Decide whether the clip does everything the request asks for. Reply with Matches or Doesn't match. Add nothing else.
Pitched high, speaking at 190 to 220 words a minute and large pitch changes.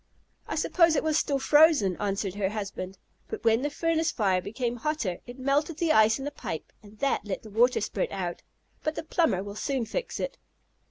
Matches